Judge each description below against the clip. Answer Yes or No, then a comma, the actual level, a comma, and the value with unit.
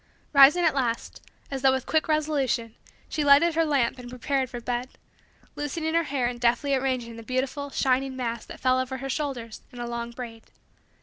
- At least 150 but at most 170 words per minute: No, average, 190 wpm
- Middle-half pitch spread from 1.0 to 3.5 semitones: Yes, average, 2.8 semitones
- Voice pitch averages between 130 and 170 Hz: No, very high, 260 Hz